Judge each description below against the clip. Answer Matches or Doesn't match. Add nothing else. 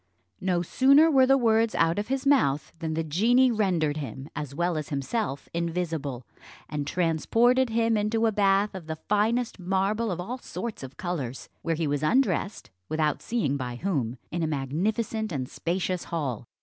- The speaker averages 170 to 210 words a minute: Matches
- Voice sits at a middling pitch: Matches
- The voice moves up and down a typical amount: Doesn't match